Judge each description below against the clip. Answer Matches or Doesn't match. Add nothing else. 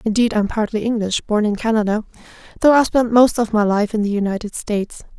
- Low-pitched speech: Doesn't match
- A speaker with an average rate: Doesn't match